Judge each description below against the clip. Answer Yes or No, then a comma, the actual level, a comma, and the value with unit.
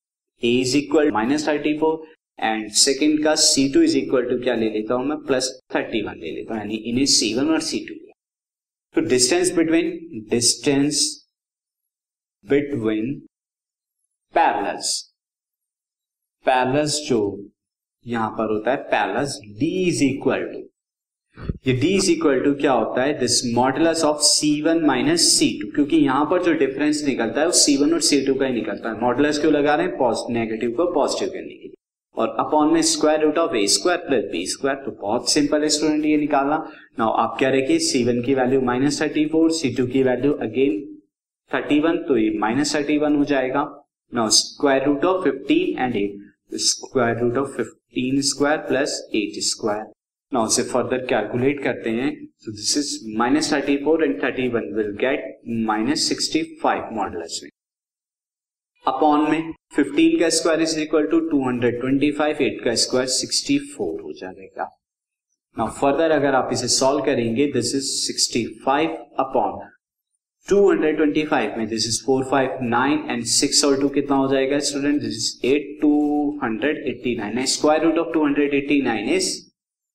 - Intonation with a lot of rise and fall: No, average, 4.1 semitones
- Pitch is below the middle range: No, medium, 145 Hz